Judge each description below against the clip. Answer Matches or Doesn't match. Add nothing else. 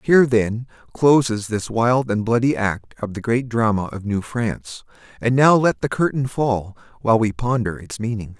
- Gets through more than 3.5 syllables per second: Matches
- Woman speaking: Doesn't match